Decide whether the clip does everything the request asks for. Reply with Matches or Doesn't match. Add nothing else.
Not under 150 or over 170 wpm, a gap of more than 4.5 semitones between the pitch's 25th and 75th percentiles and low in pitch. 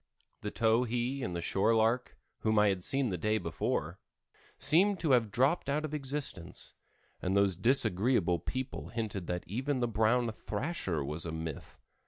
Matches